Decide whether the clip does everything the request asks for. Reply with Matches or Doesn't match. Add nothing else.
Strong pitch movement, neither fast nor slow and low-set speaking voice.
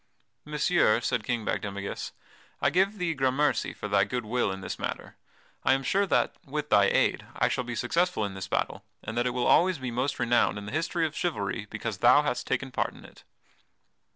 Doesn't match